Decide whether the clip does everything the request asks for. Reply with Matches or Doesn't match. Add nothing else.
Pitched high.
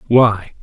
Doesn't match